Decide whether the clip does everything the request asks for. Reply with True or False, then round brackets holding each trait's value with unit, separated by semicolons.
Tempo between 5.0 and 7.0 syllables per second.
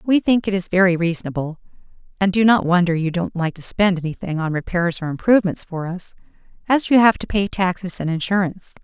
True (6.0 syllables/s)